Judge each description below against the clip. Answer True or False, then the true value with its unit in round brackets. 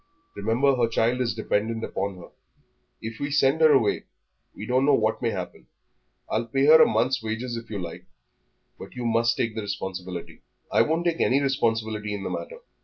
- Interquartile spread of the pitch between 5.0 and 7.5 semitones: False (3.8 semitones)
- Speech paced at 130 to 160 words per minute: False (190 wpm)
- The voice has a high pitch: False (115 Hz)